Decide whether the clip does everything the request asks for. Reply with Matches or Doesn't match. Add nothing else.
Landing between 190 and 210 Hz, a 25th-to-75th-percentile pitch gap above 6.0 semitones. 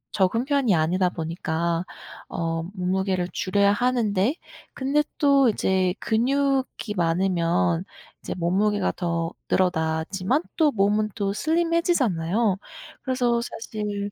Doesn't match